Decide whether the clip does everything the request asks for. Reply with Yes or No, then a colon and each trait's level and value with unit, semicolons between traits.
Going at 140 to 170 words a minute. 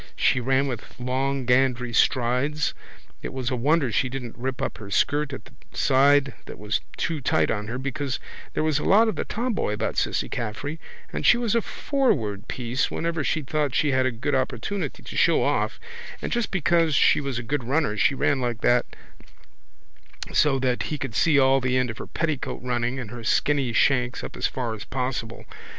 No: average, 200 wpm